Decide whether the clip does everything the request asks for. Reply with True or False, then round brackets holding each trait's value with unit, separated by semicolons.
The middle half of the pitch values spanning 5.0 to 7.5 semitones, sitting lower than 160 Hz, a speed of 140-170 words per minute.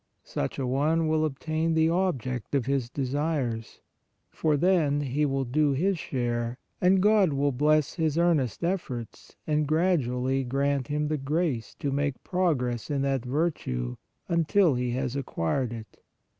False (4.1 semitones; 140 Hz; 150 wpm)